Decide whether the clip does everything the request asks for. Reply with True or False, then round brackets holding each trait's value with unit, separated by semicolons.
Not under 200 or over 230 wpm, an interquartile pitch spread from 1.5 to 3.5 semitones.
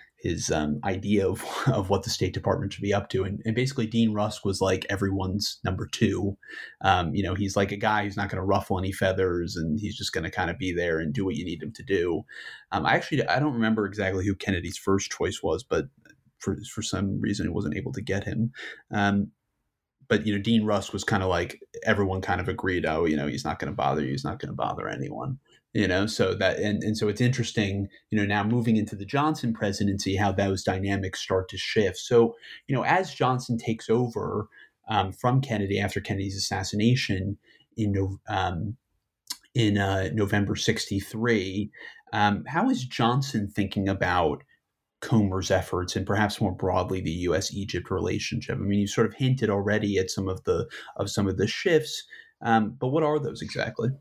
True (205 wpm; 2.5 semitones)